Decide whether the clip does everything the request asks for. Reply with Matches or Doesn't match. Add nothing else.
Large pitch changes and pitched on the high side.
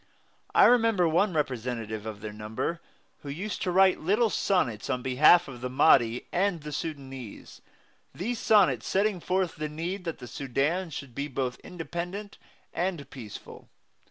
Doesn't match